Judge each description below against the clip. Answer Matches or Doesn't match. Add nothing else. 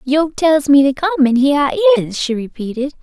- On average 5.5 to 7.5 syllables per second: Matches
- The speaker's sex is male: Doesn't match